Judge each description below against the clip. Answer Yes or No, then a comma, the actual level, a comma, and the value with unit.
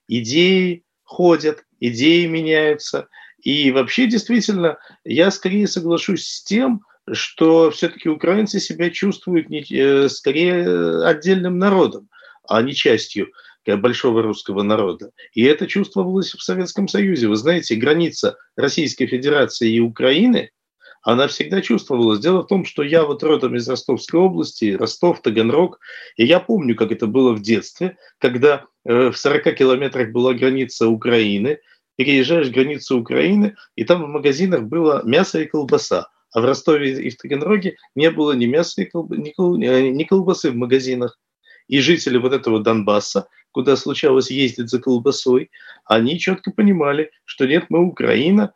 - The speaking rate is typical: Yes, average, 140 wpm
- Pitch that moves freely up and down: Yes, wide, 6.5 semitones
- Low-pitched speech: No, medium, 160 Hz